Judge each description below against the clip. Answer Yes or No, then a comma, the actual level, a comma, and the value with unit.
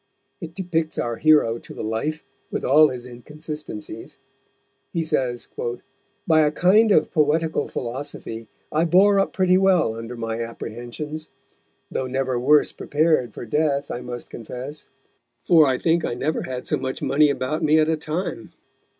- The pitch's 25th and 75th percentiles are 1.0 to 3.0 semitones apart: No, average, 4.5 semitones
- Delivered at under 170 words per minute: Yes, average, 160 wpm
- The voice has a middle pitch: Yes, medium, 150 Hz